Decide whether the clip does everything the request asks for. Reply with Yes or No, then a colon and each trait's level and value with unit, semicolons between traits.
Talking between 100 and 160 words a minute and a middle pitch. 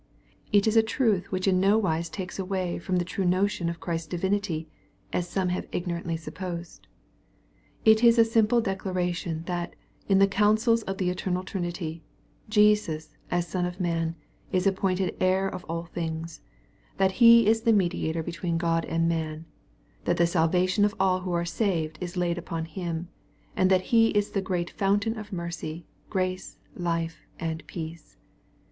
No: average, 175 wpm; medium, 180 Hz